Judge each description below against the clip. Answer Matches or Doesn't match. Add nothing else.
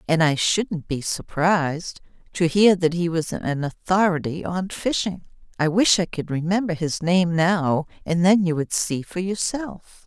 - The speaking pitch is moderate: Matches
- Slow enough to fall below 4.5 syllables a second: Matches